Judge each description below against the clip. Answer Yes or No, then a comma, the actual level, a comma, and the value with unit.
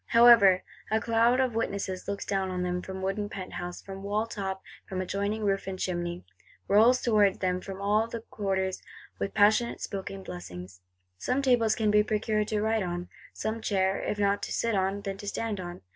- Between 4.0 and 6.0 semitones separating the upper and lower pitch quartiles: No, narrow, 2.5 semitones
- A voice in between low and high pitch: No, high, 200 Hz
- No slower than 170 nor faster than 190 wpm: Yes, average, 185 wpm